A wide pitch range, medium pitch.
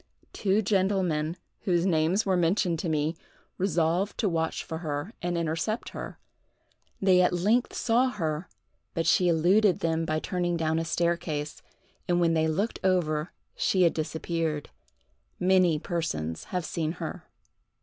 No: average, 2.7 semitones; medium, 170 Hz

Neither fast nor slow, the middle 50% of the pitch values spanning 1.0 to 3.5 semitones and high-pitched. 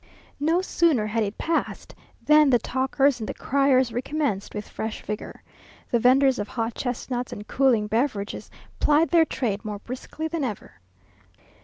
No: average, 155 wpm; average, 4.8 semitones; very high, 250 Hz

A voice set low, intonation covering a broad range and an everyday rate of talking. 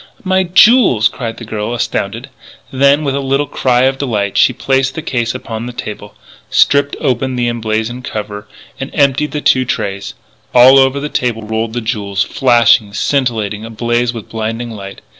No: low, 120 Hz; average, 3.5 semitones; average, 170 wpm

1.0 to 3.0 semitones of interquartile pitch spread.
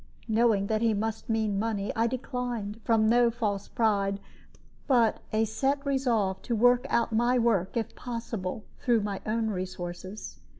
Yes: average, 2.7 semitones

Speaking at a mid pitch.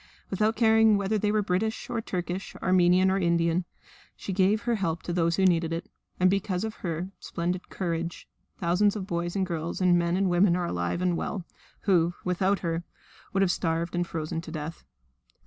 Yes: medium, 180 Hz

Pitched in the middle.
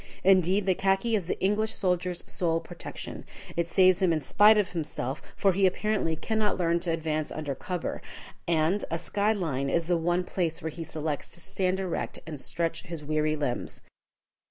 Yes: medium, 175 Hz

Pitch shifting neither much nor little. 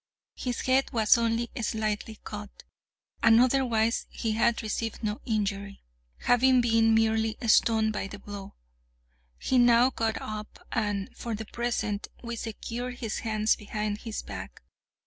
No: narrow, 1.8 semitones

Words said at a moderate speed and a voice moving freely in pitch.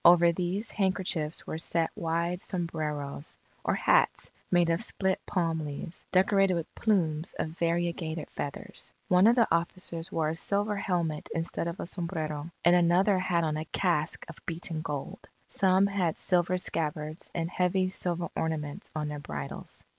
No: average, 155 wpm; narrow, 2.6 semitones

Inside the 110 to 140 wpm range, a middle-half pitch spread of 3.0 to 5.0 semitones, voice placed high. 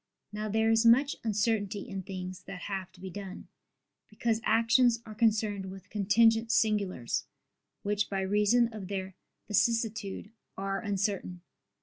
No: slow, 135 wpm; narrow, 2.5 semitones; high, 210 Hz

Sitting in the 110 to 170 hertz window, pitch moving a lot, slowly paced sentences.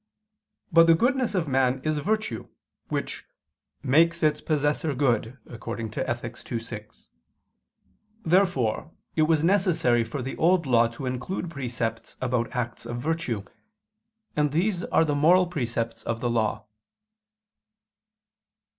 Yes: medium, 140 Hz; wide, 5.7 semitones; slow, 125 wpm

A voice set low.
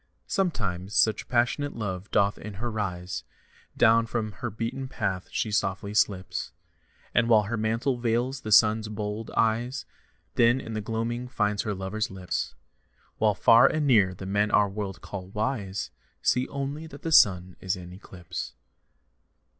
Yes: low, 110 Hz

